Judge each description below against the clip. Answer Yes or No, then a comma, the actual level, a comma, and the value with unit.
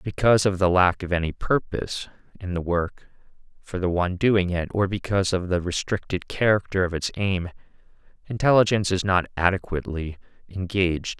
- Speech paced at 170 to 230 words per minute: No, average, 155 wpm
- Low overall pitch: Yes, very low, 95 Hz